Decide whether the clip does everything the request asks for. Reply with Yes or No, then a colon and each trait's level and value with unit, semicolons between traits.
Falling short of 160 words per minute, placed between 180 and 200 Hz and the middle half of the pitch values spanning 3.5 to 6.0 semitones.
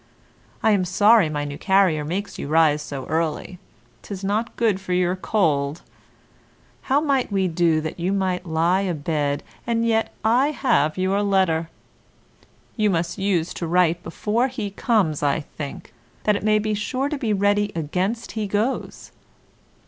No: average, 165 wpm; high, 190 Hz; average, 4.7 semitones